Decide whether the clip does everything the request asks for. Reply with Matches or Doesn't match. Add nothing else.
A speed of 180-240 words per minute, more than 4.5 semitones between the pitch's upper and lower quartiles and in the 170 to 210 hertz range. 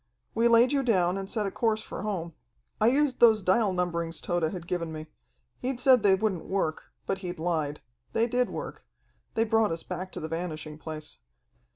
Matches